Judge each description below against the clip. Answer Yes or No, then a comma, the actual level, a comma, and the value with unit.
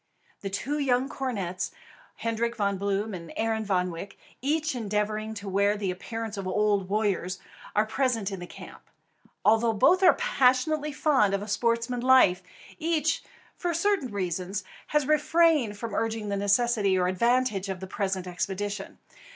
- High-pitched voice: Yes, high, 215 Hz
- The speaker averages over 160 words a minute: No, average, 155 wpm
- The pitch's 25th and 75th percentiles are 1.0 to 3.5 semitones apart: No, average, 4.5 semitones